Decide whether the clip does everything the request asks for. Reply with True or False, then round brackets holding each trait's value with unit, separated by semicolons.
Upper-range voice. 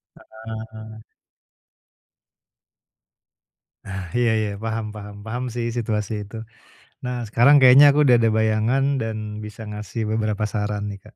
False (110 Hz)